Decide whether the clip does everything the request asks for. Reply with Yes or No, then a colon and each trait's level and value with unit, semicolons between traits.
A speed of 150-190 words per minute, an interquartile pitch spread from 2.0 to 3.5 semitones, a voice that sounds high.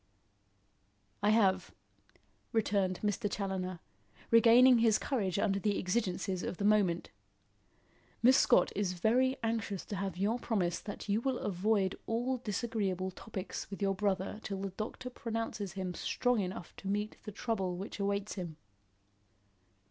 No: average, 140 wpm; average, 3.1 semitones; high, 200 Hz